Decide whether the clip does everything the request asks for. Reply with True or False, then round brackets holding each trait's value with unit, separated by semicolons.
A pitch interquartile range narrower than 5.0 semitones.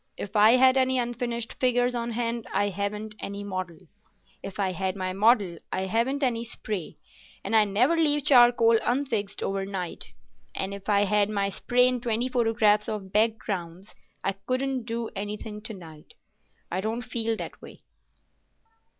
True (3.4 semitones)